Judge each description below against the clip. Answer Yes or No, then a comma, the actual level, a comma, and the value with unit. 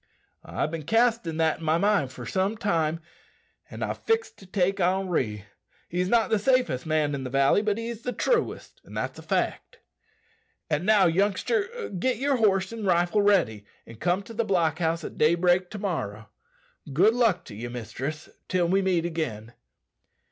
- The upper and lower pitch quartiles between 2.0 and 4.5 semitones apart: No, average, 5.1 semitones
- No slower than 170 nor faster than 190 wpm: Yes, average, 175 wpm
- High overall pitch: No, medium, 180 Hz